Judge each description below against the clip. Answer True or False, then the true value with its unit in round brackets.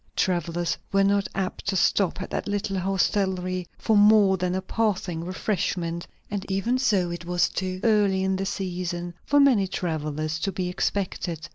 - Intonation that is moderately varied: False (2.3 semitones)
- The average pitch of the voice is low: False (190 Hz)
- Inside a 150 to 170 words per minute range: True (165 wpm)